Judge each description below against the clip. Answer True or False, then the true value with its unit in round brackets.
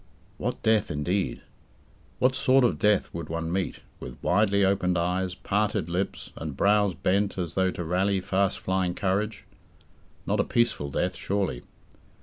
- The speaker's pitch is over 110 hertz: False (95 Hz)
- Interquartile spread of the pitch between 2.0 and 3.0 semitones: True (2.6 semitones)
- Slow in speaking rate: False (150 wpm)